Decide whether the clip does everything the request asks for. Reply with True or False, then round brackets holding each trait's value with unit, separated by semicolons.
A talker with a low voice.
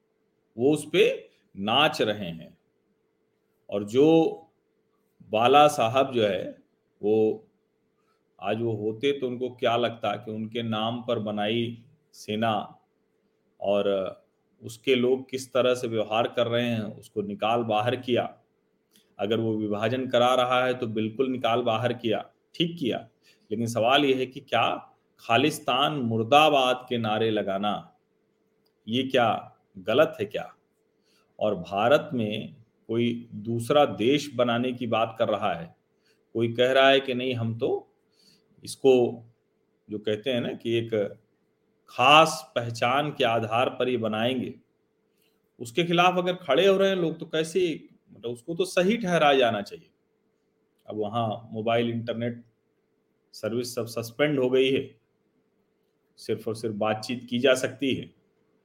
True (120 Hz)